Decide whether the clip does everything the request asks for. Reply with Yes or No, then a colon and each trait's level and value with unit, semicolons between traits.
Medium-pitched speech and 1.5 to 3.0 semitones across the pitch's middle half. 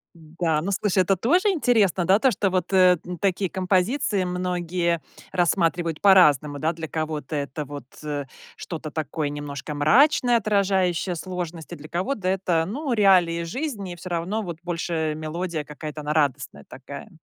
No: medium, 175 Hz; average, 3.7 semitones